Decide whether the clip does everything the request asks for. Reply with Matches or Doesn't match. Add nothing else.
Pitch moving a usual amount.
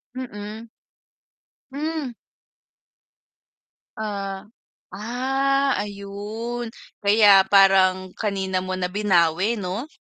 Matches